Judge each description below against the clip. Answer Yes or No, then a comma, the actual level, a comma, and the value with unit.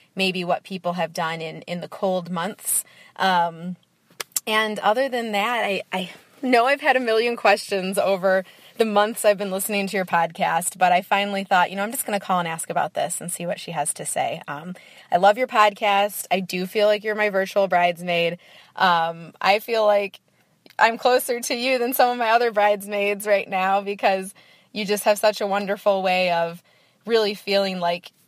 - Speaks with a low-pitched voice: No, high, 200 Hz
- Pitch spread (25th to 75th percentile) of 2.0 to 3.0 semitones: Yes, average, 2.7 semitones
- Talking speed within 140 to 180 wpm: No, average, 200 wpm